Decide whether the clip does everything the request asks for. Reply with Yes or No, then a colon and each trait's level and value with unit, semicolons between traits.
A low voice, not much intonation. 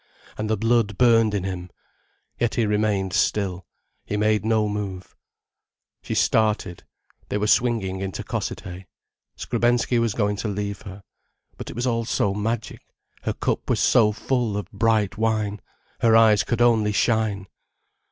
Yes: low, 105 Hz; narrow, 2.0 semitones